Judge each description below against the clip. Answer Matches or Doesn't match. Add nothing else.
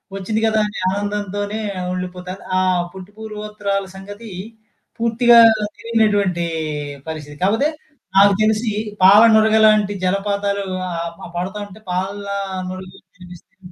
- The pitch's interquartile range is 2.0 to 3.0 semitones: Matches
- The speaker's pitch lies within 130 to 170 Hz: Doesn't match